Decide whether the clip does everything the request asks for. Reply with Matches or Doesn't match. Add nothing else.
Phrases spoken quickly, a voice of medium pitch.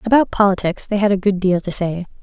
Doesn't match